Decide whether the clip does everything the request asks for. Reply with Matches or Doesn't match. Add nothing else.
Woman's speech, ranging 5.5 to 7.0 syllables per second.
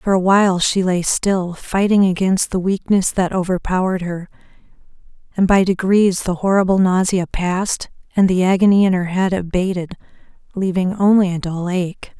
Doesn't match